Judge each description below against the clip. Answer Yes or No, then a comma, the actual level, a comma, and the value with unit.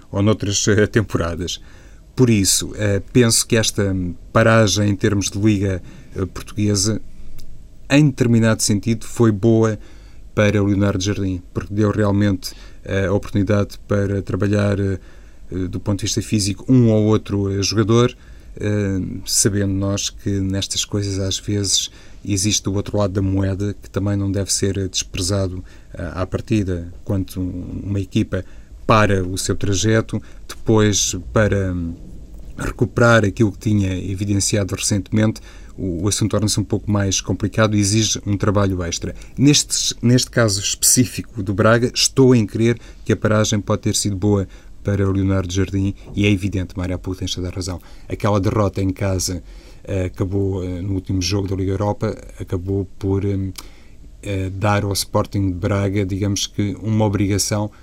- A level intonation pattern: Yes, narrow, 2.1 semitones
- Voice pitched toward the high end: No, low, 100 Hz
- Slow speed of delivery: No, average, 145 wpm